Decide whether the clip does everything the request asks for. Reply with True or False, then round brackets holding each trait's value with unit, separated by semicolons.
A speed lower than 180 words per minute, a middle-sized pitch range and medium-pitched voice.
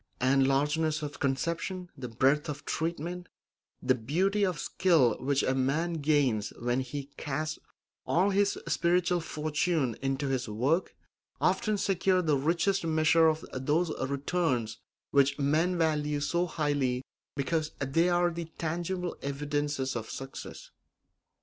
True (135 wpm; 4.1 semitones; 150 Hz)